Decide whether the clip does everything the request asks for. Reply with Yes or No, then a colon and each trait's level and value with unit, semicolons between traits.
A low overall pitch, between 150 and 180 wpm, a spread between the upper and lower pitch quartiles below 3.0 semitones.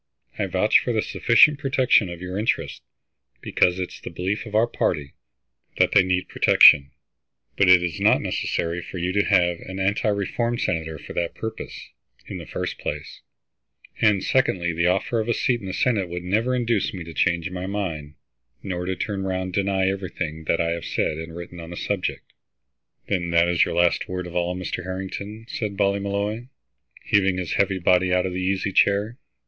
No: very low, 95 Hz; average, 195 wpm; narrow, 2.6 semitones